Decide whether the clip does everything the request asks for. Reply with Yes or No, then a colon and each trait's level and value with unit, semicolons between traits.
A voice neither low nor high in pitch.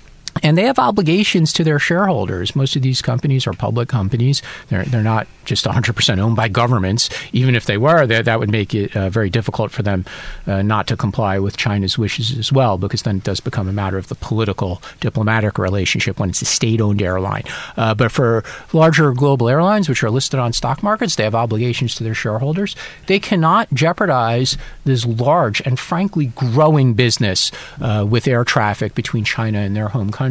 No: low, 120 Hz